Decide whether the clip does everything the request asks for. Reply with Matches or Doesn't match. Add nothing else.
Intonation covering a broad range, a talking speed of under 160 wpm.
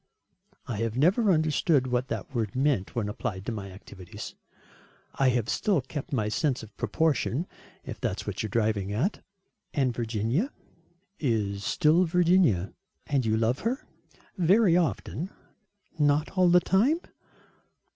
Matches